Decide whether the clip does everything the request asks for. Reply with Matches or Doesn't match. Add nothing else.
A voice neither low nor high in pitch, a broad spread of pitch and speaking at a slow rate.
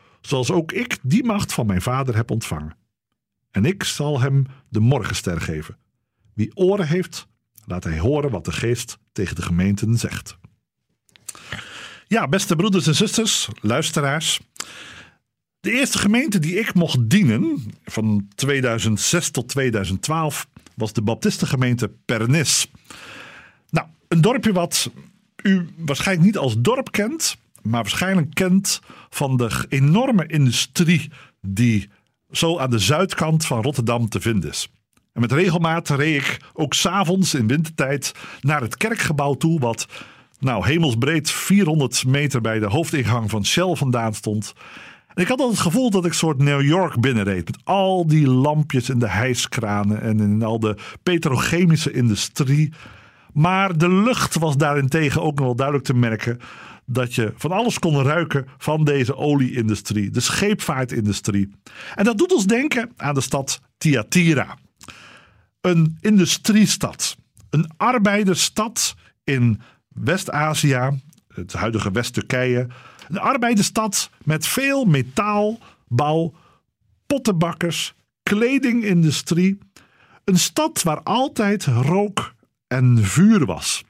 Matches